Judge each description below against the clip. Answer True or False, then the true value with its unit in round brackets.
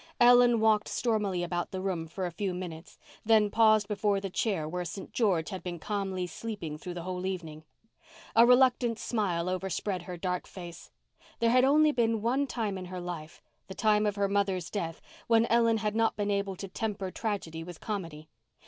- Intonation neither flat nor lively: True (3.8 semitones)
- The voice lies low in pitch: False (200 Hz)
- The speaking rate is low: False (185 wpm)